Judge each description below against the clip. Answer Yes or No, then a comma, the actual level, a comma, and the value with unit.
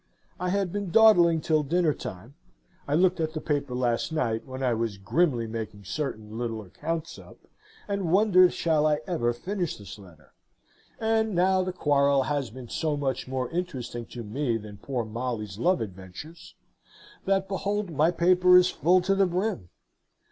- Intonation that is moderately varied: No, wide, 7.4 semitones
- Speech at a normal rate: Yes, average, 170 wpm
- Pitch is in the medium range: Yes, medium, 150 Hz